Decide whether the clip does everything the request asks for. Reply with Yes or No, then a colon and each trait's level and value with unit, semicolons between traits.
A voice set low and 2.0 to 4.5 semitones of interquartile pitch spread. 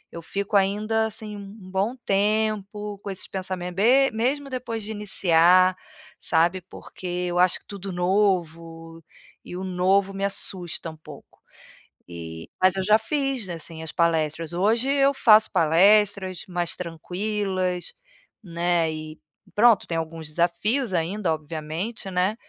No: high, 190 Hz; average, 3.8 semitones